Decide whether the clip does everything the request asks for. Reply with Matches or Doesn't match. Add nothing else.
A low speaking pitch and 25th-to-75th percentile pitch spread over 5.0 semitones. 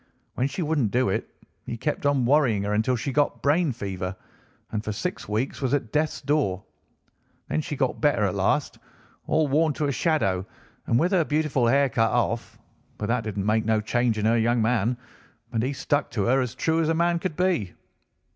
Matches